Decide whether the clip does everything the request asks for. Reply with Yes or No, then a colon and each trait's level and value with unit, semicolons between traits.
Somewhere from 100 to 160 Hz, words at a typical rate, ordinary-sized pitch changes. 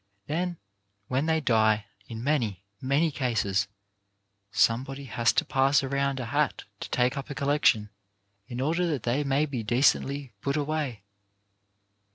Yes: low, 135 Hz; average, 155 wpm; average, 4.2 semitones